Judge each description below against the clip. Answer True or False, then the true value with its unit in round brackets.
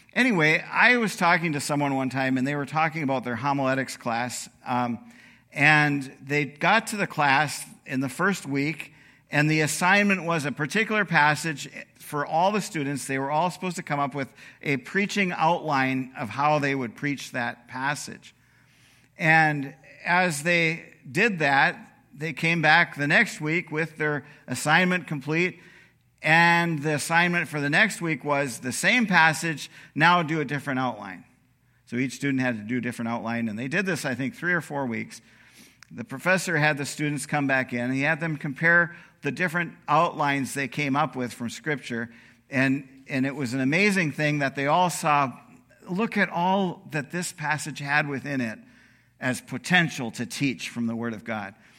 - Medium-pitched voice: True (145 Hz)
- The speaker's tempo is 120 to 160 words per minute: False (180 wpm)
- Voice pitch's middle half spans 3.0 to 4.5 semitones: True (4.0 semitones)